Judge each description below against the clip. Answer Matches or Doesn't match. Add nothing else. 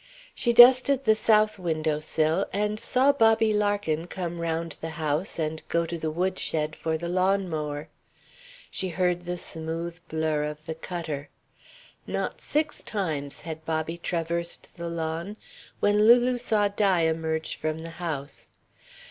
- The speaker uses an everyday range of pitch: Matches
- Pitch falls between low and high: Matches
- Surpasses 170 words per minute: Doesn't match